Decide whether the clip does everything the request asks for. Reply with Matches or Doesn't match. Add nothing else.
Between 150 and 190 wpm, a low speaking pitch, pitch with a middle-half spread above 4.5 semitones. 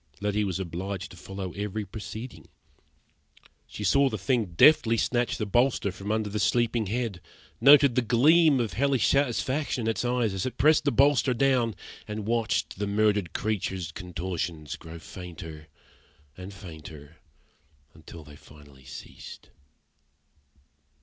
Doesn't match